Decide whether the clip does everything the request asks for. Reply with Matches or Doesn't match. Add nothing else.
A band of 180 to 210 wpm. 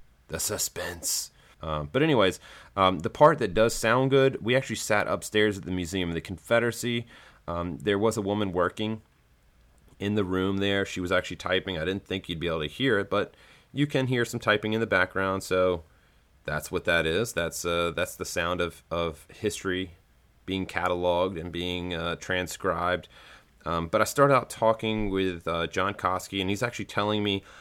Matches